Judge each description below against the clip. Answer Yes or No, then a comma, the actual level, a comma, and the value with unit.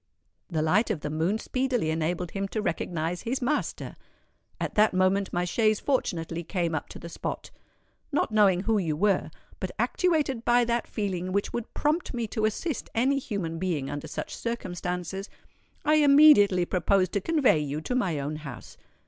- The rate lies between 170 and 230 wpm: Yes, average, 175 wpm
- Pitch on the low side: No, high, 195 Hz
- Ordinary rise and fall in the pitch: No, wide, 5.9 semitones